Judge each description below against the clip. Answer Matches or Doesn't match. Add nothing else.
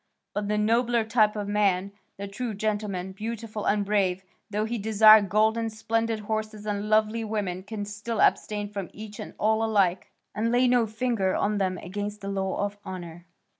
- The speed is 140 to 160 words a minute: Doesn't match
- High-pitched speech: Matches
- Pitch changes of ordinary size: Doesn't match